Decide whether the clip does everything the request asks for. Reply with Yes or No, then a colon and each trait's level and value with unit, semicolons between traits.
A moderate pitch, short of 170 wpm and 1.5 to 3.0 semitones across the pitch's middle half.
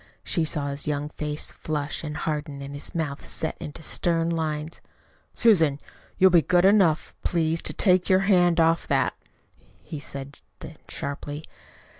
Yes: medium, 155 Hz; average, 155 wpm; average, 2.7 semitones